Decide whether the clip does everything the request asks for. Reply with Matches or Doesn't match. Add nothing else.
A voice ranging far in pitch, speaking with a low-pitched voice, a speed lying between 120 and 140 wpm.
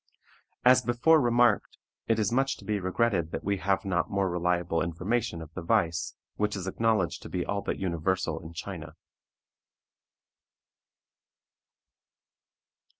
Doesn't match